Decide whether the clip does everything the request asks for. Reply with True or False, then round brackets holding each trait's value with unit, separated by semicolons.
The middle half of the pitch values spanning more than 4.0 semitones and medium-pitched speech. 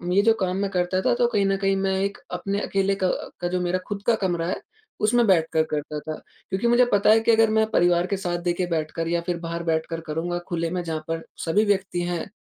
False (3.0 semitones; 180 Hz)